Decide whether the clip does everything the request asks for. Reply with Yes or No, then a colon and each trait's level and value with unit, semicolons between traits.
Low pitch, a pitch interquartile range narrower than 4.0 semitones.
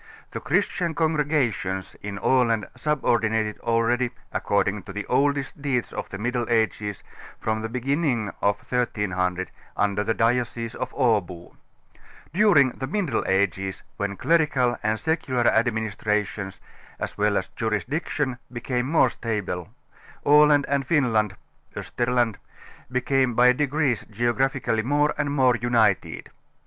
No: low, 120 Hz; average, 4.4 semitones